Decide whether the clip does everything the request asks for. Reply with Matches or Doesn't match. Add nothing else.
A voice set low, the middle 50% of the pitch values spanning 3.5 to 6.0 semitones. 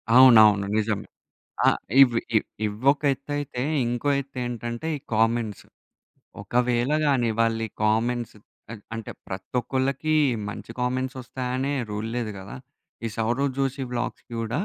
Doesn't match